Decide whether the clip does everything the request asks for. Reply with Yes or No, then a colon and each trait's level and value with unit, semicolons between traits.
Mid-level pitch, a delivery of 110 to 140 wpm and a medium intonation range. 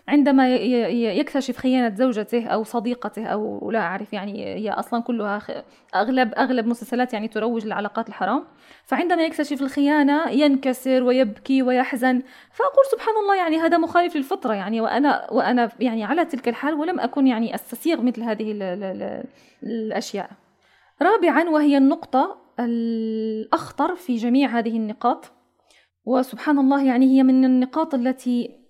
No: very high, 255 Hz; average, 130 wpm; average, 3.7 semitones